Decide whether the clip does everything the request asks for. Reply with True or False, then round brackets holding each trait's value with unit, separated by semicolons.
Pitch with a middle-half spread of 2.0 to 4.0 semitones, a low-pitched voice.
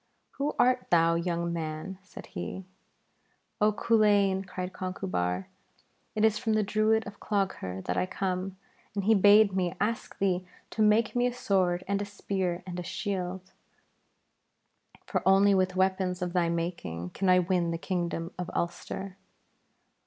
False (2.6 semitones; 190 Hz)